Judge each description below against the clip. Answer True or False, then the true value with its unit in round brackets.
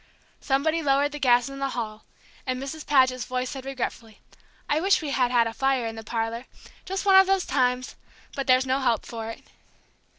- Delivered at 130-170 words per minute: False (200 wpm)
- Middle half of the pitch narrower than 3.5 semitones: True (2.6 semitones)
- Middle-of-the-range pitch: False (260 Hz)